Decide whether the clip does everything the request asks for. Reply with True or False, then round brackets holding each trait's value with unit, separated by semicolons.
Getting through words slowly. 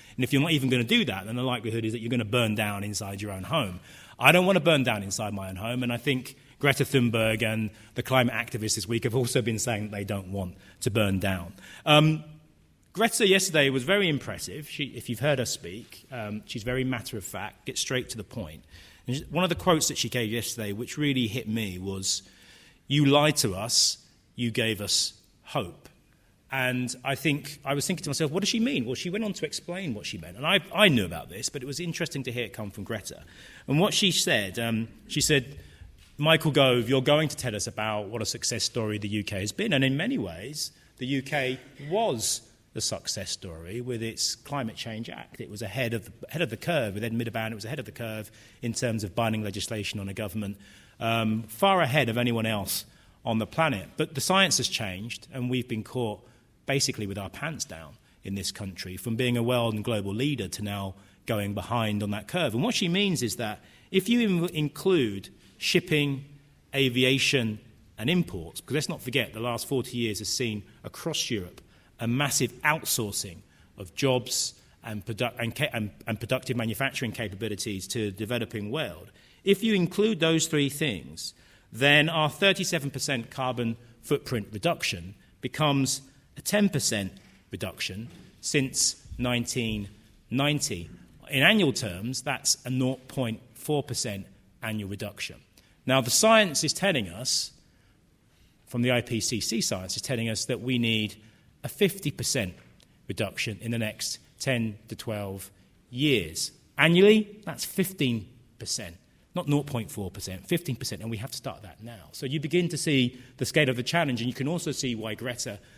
False (190 wpm)